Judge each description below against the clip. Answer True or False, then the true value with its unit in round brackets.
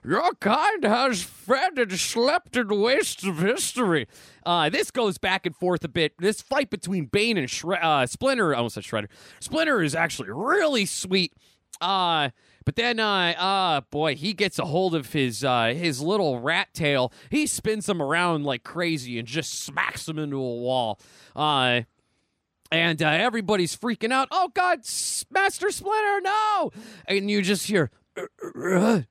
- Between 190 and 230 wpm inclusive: False (165 wpm)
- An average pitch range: False (6.8 semitones)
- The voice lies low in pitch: False (185 Hz)